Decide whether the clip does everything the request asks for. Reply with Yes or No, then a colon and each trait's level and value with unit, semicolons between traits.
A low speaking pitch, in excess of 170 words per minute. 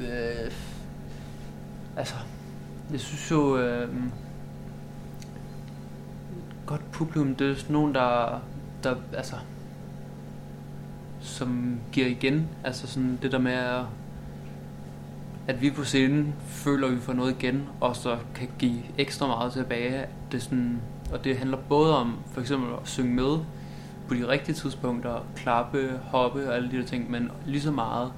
No: low, 125 Hz; slow, 145 wpm